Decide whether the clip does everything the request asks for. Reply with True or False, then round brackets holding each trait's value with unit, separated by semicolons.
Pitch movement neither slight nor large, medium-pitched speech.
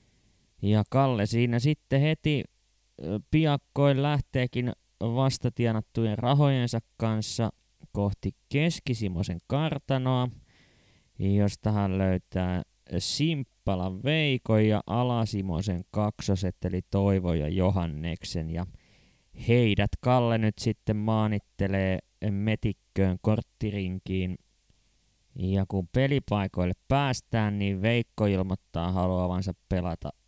False (4.5 semitones; 105 Hz)